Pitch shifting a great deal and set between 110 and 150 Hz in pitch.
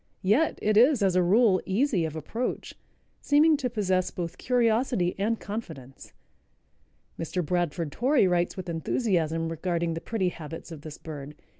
No: wide, 5.7 semitones; medium, 185 Hz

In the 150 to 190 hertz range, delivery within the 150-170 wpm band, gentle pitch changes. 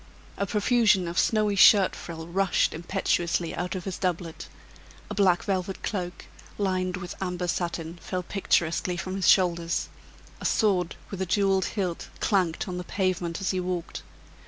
Yes: medium, 185 Hz; average, 160 wpm; narrow, 2.0 semitones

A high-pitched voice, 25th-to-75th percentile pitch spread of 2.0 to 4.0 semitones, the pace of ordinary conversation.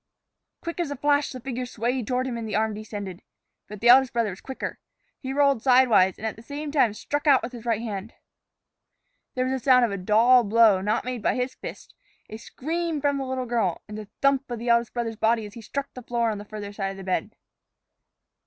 No: high, 235 Hz; average, 3.5 semitones; fast, 235 wpm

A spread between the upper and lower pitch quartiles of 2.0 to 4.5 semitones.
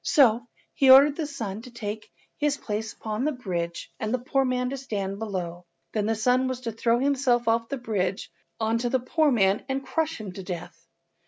Yes: average, 3.9 semitones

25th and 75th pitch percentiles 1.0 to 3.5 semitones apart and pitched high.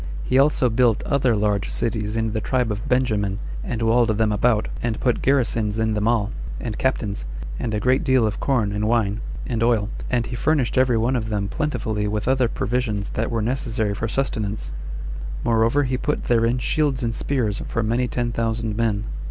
No: average, 2.8 semitones; low, 115 Hz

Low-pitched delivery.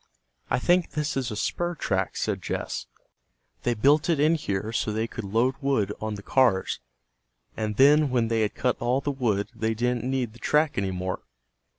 Yes: low, 120 Hz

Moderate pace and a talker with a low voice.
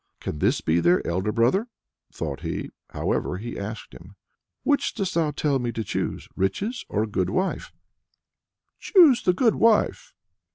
Yes: average, 160 wpm; low, 120 Hz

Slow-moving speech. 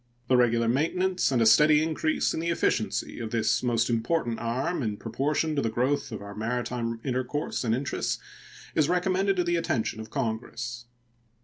No: average, 175 wpm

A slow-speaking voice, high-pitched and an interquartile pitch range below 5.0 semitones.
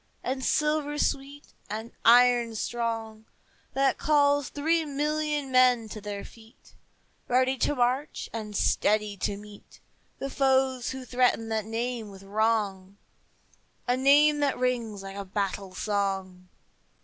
Yes: slow, 130 wpm; high, 240 Hz; average, 4.5 semitones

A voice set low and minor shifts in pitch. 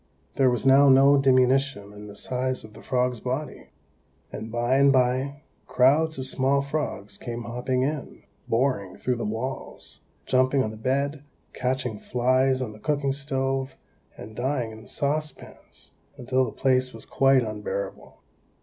Yes: low, 130 Hz; narrow, 2.3 semitones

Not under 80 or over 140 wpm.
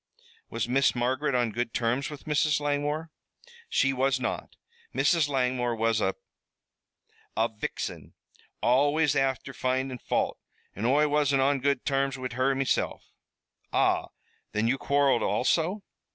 Yes: slow, 135 wpm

